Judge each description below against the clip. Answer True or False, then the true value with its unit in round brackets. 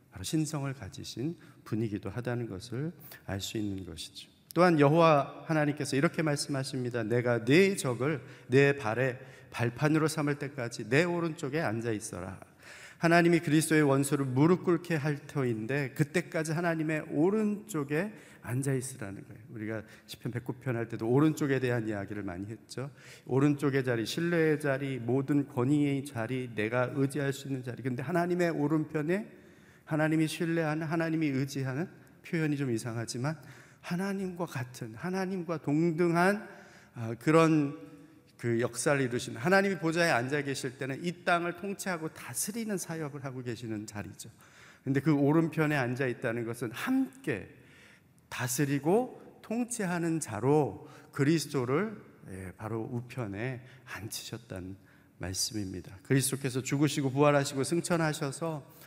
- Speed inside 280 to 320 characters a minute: False (330 characters per minute)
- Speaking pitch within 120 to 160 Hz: True (140 Hz)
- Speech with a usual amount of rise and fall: True (4.7 semitones)